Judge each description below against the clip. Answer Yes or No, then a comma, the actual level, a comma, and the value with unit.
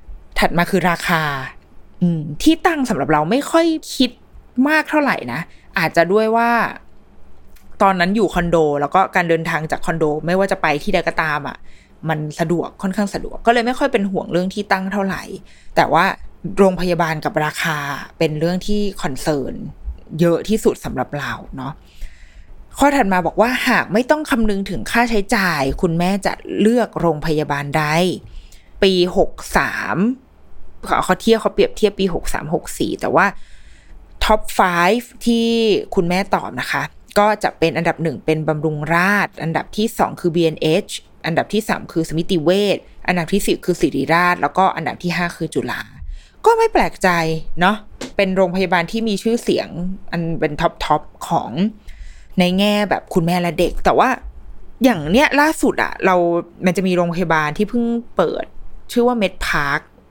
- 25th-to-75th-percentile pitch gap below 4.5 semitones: No, average, 4.8 semitones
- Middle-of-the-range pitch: Yes, medium, 180 Hz